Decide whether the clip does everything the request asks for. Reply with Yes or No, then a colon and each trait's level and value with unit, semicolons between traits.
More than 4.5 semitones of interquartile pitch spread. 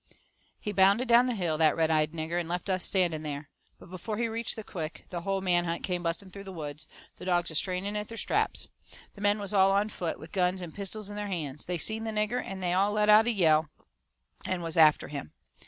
No: average, 3.9 semitones